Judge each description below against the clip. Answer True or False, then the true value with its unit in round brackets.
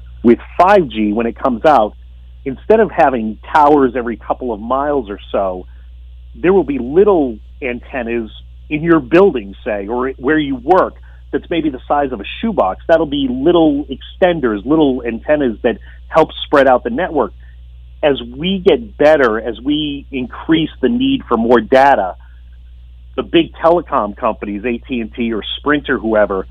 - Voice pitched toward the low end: True (125 Hz)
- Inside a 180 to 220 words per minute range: False (155 wpm)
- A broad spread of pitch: True (9.0 semitones)